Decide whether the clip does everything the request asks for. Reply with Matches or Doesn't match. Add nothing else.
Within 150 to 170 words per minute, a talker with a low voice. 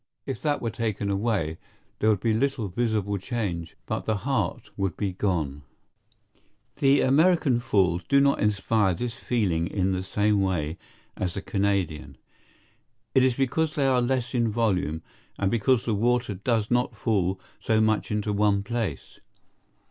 Matches